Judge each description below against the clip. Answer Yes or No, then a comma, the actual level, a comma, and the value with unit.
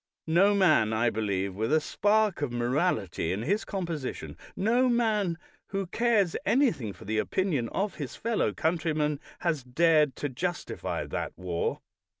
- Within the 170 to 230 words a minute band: No, average, 150 wpm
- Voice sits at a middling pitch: Yes, medium, 160 Hz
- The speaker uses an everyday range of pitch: No, wide, 8.6 semitones